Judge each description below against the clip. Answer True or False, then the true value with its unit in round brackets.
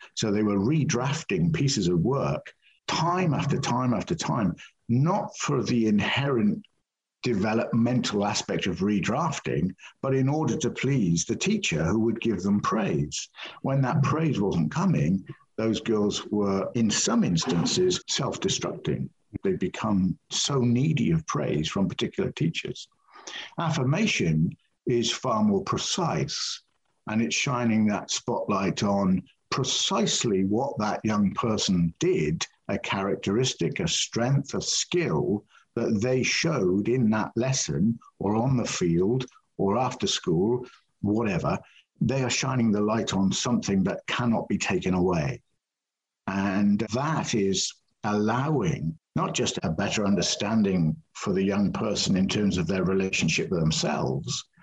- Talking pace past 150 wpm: False (135 wpm)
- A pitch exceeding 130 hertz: False (115 Hz)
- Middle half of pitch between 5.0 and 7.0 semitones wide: True (5.5 semitones)